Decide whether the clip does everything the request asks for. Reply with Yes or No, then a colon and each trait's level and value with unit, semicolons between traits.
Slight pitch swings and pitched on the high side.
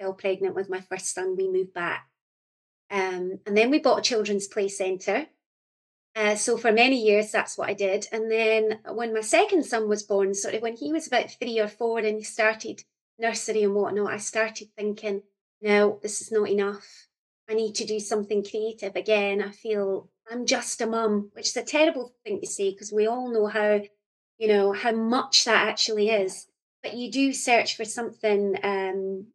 Yes: narrow, 2.0 semitones; high, 210 Hz